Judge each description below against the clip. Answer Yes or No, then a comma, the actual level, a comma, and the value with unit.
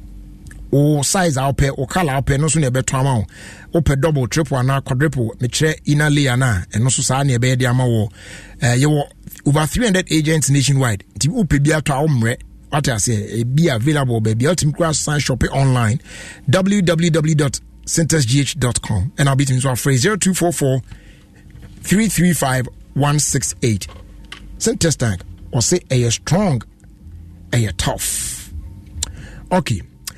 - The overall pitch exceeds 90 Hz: Yes, low, 135 Hz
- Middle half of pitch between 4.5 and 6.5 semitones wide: Yes, average, 5.1 semitones